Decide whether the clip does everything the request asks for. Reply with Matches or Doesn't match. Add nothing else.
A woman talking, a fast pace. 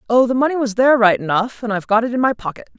Matches